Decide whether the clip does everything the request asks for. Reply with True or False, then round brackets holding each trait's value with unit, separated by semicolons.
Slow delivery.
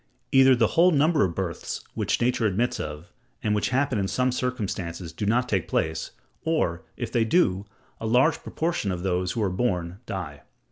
False (185 wpm)